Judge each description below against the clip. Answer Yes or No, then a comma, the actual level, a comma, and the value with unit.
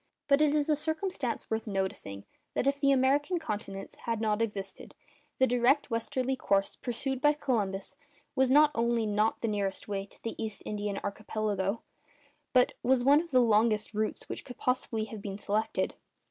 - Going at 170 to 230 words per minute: Yes, average, 175 wpm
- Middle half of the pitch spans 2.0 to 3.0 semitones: No, average, 4.3 semitones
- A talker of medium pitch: No, high, 230 Hz